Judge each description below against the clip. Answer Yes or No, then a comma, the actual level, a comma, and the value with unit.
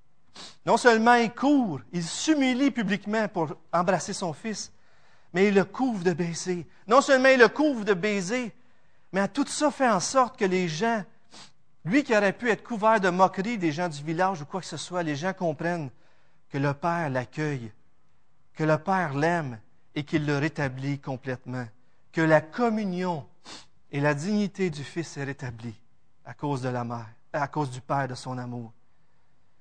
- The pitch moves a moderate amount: No, wide, 6.8 semitones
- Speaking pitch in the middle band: Yes, medium, 175 Hz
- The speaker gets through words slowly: No, average, 180 wpm